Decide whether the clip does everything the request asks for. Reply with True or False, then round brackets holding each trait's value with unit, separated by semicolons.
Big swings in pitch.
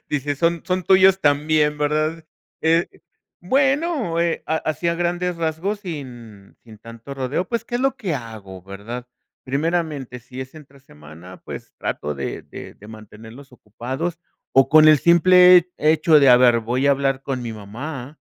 True (5.8 semitones)